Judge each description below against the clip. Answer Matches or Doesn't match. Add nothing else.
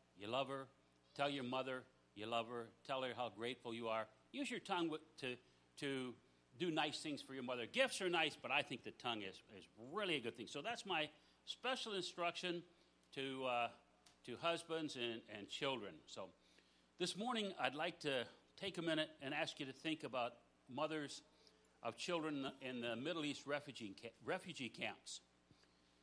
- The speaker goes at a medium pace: Matches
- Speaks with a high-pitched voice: Doesn't match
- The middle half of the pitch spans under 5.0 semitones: Doesn't match